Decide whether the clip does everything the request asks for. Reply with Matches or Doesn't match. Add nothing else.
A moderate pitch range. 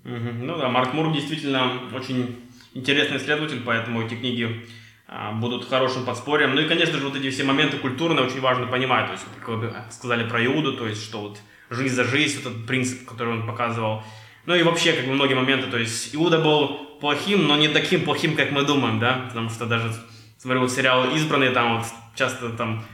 Matches